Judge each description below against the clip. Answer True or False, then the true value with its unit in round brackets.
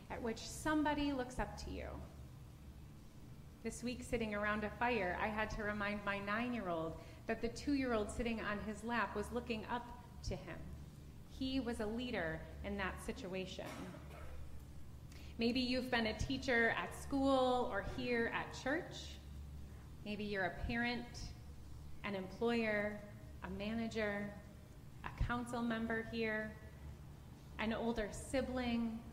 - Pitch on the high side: True (220 Hz)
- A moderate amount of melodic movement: True (4.0 semitones)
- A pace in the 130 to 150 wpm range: True (140 wpm)